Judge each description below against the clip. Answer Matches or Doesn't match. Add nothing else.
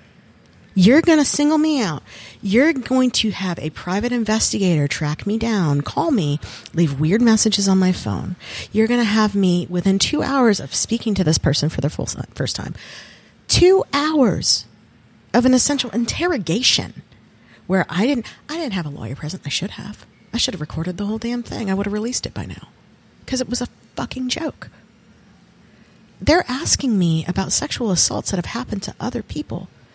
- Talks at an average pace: Matches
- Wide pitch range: Matches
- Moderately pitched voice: Doesn't match